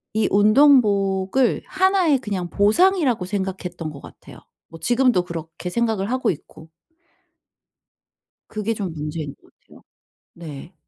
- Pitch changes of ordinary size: No, wide, 5.9 semitones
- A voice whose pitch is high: Yes, high, 200 Hz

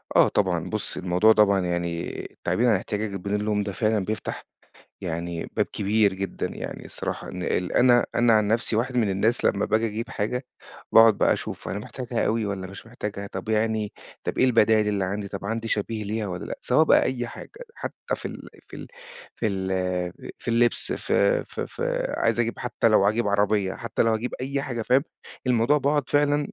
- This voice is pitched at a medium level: No, low, 110 Hz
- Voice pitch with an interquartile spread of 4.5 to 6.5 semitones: No, average, 3.0 semitones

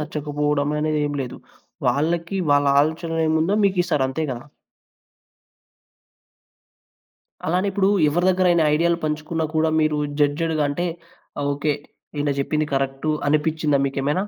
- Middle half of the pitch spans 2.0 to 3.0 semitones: Yes, narrow, 2.5 semitones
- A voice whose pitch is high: No, medium, 155 Hz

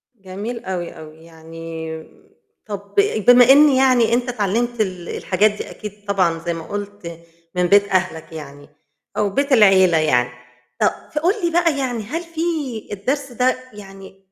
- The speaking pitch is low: No, high, 200 Hz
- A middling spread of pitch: No, wide, 6.3 semitones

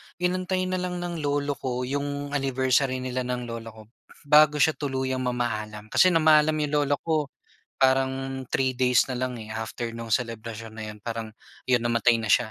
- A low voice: Yes, low, 130 Hz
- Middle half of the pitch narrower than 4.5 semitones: Yes, average, 3.8 semitones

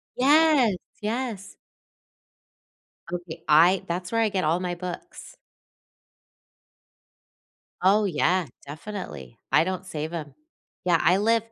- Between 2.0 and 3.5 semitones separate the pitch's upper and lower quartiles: No, average, 4.1 semitones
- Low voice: No, medium, 185 Hz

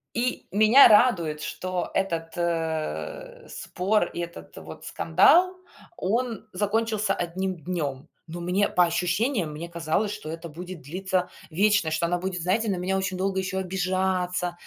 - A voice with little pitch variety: No, average, 3.4 semitones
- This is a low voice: No, medium, 185 Hz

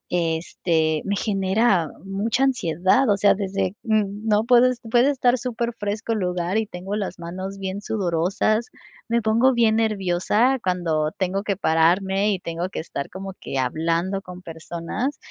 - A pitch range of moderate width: Yes, average, 4.0 semitones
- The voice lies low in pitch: No, high, 195 Hz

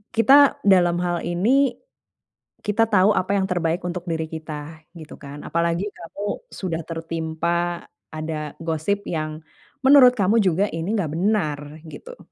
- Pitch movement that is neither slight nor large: Yes, average, 4.0 semitones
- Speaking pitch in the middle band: Yes, medium, 175 Hz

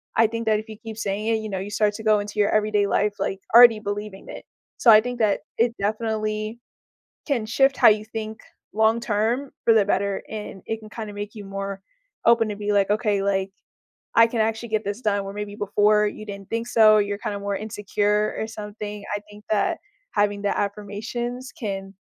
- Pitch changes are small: Yes, narrow, 1.5 semitones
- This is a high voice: Yes, high, 210 Hz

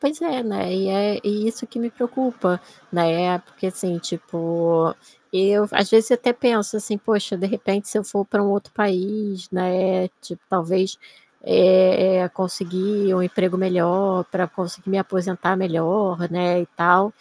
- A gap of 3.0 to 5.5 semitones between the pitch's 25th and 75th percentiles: No, narrow, 2.4 semitones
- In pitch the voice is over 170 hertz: Yes, high, 190 Hz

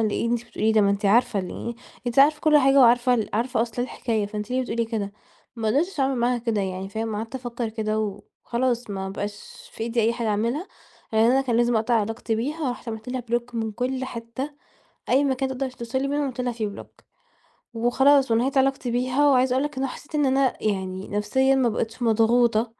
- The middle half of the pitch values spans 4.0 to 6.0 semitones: No, average, 3.0 semitones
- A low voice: No, high, 240 Hz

